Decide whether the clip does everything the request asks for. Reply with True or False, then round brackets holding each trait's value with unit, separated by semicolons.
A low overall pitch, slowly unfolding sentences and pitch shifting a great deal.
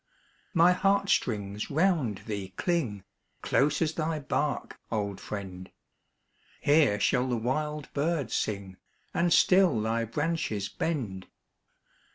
True (130 Hz; 115 wpm; 7.8 semitones)